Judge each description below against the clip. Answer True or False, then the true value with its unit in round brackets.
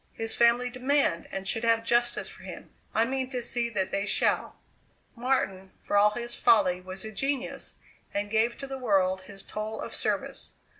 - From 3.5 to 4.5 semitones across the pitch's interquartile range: True (3.8 semitones)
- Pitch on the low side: False (225 Hz)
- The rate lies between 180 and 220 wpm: True (185 wpm)